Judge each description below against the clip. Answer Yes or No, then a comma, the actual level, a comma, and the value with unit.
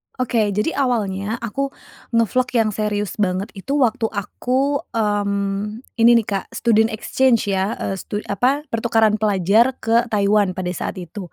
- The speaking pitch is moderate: No, high, 215 Hz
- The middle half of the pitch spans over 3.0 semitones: No, average, 2.7 semitones